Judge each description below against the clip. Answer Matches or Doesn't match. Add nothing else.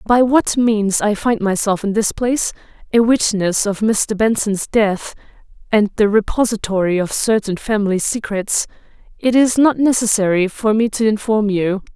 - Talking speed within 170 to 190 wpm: Doesn't match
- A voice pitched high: Matches